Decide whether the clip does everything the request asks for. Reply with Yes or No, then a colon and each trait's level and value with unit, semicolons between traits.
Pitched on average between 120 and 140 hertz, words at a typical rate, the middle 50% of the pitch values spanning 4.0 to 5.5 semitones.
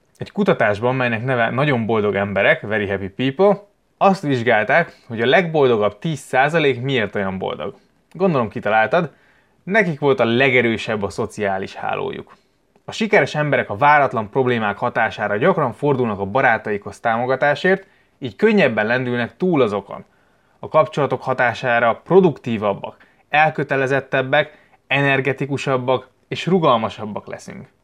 Yes: low, 130 Hz; average, 115 wpm; average, 4.7 semitones